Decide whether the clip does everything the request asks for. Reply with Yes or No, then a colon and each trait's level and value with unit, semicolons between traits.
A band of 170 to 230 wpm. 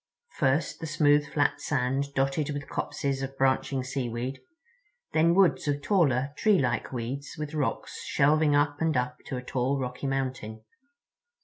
No: average, 140 wpm